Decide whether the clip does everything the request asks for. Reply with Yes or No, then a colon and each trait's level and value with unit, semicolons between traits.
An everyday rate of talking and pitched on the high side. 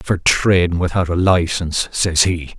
No: average, 160 wpm; very low, 90 Hz